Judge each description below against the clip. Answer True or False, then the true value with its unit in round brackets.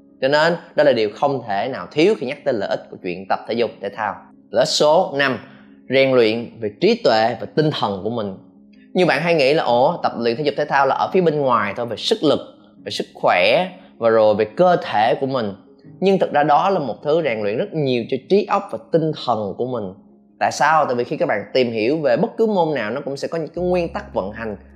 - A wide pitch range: True (7.2 semitones)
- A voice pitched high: False (135 Hz)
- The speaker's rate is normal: False (265 wpm)